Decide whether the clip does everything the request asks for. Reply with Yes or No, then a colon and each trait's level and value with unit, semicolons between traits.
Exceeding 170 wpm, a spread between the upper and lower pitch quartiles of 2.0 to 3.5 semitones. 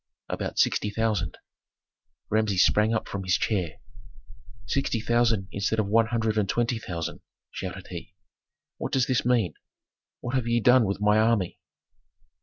No: average, 150 wpm; average, 2.9 semitones